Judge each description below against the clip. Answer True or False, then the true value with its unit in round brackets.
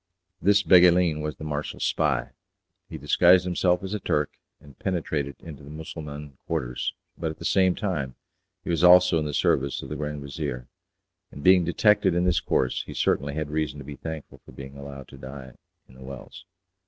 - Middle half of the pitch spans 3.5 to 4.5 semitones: True (4.0 semitones)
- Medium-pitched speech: False (75 Hz)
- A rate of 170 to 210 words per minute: True (190 wpm)